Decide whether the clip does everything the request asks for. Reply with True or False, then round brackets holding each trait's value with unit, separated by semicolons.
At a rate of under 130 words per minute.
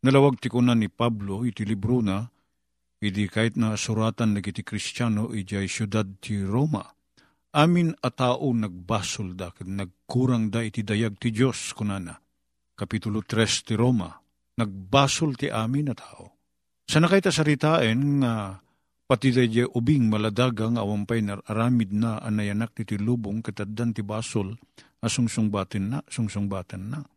False (140 wpm)